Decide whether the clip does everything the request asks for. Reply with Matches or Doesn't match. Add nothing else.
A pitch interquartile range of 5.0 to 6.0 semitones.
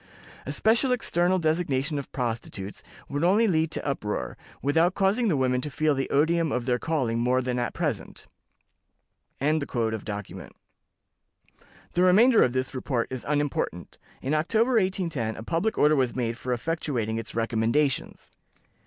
Matches